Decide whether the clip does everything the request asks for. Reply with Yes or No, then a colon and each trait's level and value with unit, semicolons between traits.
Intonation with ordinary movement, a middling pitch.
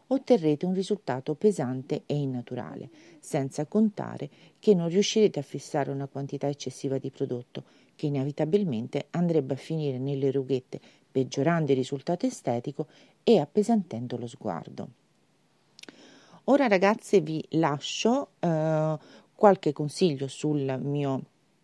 No: wide, 5.7 semitones; medium, 150 Hz